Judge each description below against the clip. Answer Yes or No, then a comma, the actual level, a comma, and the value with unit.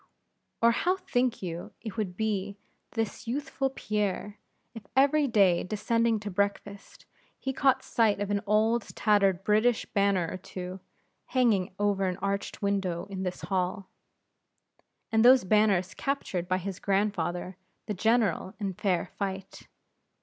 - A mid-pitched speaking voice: No, high, 205 Hz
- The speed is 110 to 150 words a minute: Yes, average, 140 wpm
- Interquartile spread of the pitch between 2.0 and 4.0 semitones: Yes, average, 3.2 semitones